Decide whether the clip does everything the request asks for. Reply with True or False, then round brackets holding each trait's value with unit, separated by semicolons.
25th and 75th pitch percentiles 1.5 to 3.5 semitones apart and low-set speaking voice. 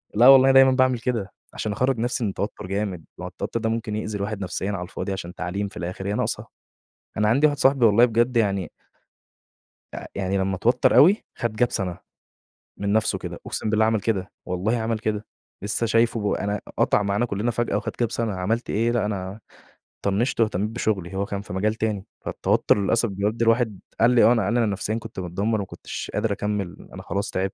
True (2.8 semitones; 105 Hz)